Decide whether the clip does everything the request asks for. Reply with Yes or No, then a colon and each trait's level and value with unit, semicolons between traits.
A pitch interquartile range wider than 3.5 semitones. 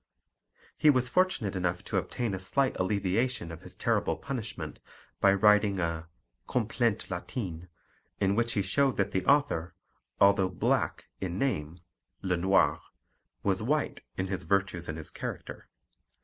Yes: average, 4.7 semitones